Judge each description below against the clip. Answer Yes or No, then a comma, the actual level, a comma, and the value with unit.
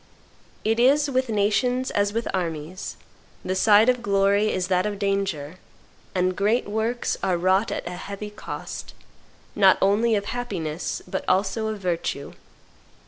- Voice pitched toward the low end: No, high, 200 Hz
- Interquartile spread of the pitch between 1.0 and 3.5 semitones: Yes, average, 3.2 semitones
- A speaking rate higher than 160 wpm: No, average, 145 wpm